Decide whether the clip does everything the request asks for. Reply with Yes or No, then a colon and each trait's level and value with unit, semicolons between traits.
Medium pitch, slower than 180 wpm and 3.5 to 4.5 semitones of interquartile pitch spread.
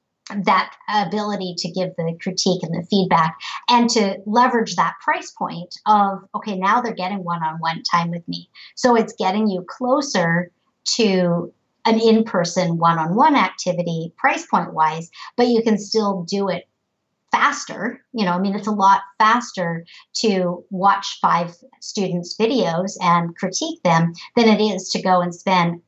No: high, 195 Hz; average, 165 wpm; average, 4.1 semitones